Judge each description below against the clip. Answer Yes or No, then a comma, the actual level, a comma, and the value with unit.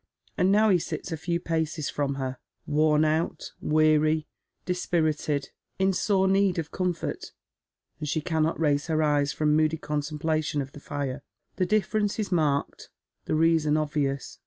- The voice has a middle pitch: Yes, medium, 155 Hz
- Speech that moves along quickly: No, average, 160 wpm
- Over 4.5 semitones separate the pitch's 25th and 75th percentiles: No, narrow, 2.6 semitones